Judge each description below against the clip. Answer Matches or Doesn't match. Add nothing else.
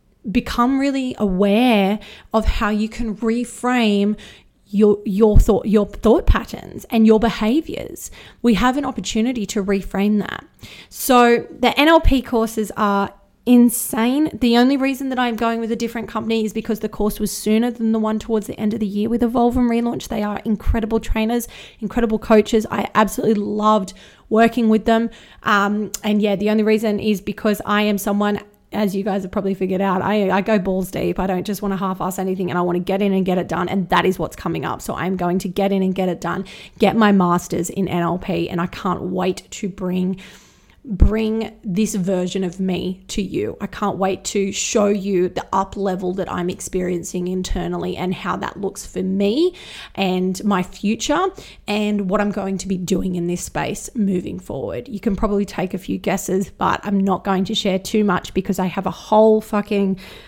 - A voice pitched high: Matches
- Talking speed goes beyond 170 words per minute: Matches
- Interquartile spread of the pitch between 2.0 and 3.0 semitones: Matches